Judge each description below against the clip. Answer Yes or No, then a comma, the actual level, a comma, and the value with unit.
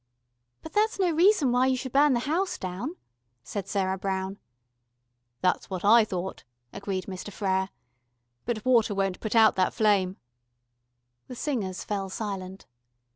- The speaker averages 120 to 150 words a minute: Yes, average, 145 wpm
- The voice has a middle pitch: No, high, 205 Hz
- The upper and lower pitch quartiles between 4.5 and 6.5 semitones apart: Yes, average, 5.2 semitones